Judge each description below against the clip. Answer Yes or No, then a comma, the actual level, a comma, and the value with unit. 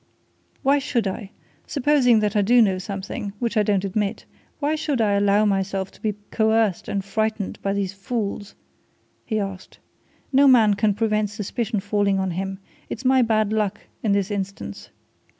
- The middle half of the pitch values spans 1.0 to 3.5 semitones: Yes, narrow, 2.4 semitones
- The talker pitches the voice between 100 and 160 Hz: No, high, 210 Hz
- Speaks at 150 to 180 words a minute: Yes, average, 170 wpm